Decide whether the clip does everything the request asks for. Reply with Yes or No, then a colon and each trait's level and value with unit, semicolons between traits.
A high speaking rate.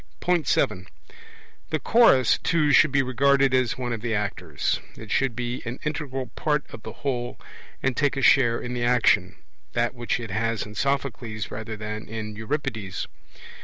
No: average, 165 wpm